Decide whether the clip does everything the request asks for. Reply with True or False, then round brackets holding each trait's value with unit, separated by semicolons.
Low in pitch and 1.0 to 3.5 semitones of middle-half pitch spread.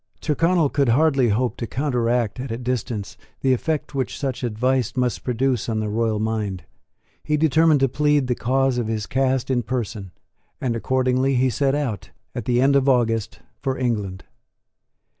True (125 Hz; 2.9 semitones)